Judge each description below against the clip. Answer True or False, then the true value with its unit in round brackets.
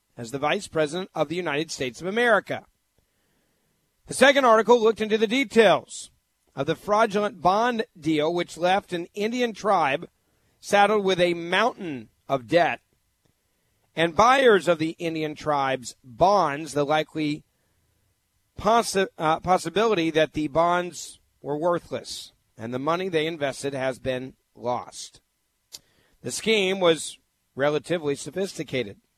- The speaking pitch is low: False (160 Hz)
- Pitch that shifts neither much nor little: False (5.9 semitones)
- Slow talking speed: True (130 wpm)